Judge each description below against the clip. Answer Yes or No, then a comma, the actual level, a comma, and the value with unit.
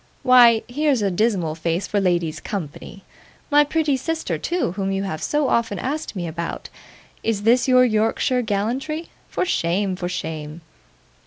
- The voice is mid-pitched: No, high, 210 Hz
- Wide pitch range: Yes, wide, 6.3 semitones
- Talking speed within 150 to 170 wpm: Yes, average, 155 wpm